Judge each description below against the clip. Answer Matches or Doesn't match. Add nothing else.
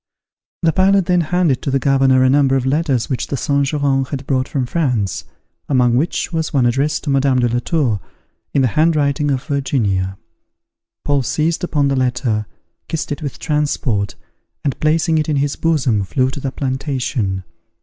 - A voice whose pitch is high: Doesn't match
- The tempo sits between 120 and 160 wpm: Doesn't match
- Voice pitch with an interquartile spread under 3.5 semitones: Matches